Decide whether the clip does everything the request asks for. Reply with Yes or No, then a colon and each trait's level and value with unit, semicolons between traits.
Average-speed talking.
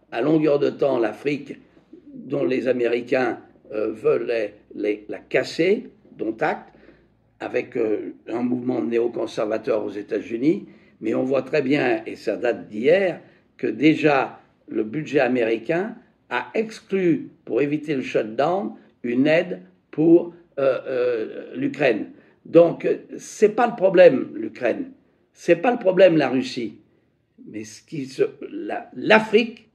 No: slow, 140 wpm